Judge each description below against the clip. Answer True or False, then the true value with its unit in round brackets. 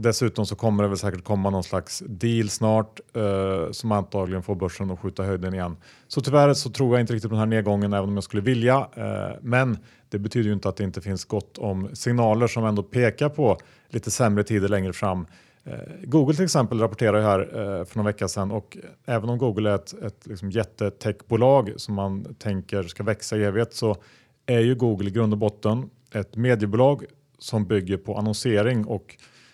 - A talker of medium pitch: False (105 Hz)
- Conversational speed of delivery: False (205 wpm)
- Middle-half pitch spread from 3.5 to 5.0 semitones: False (3.0 semitones)